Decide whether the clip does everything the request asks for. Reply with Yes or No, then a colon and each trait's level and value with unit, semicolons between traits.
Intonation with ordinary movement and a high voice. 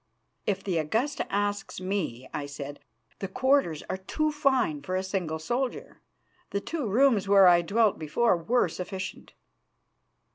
No: wide, 5.9 semitones; high, 195 Hz